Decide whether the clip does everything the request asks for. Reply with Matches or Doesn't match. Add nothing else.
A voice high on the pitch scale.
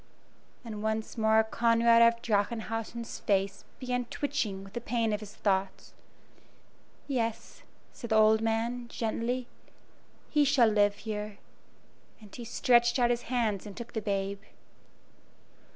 Matches